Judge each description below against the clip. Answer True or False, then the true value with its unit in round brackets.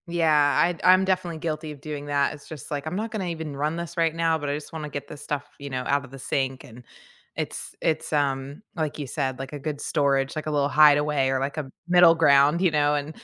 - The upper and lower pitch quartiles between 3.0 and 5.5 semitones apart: False (2.5 semitones)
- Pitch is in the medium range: True (150 Hz)